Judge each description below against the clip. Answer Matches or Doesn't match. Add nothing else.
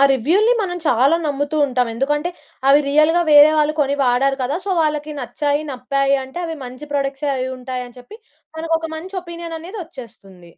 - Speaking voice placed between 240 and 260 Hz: Doesn't match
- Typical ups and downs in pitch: Matches